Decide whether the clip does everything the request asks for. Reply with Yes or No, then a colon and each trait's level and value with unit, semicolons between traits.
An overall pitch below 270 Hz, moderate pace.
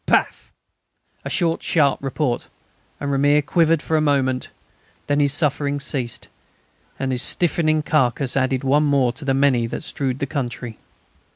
Yes: medium, 140 Hz; average, 155 wpm